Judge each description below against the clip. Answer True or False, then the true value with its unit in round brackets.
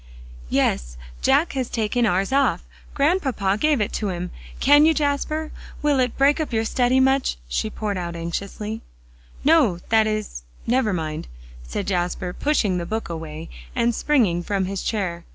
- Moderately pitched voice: False (215 Hz)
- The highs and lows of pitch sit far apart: True (7.1 semitones)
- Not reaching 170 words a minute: True (160 wpm)